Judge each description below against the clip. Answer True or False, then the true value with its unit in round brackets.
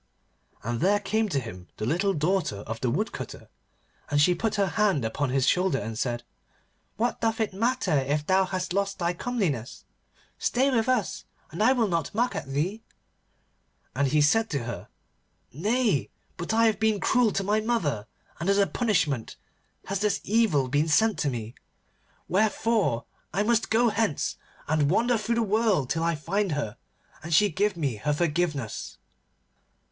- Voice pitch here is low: False (185 Hz)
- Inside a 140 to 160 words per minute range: False (170 wpm)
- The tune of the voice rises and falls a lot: True (7.2 semitones)